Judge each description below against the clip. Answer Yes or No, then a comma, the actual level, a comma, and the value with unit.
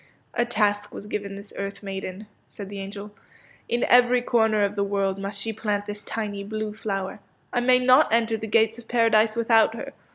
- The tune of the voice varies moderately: No, narrow, 2.2 semitones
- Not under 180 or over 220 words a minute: Yes, average, 200 wpm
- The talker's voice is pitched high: Yes, high, 215 Hz